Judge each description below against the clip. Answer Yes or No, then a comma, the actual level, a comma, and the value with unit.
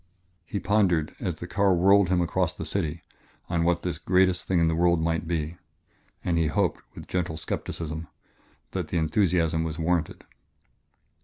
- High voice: No, very low, 85 Hz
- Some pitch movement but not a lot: No, narrow, 2.0 semitones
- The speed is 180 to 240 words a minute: No, average, 165 wpm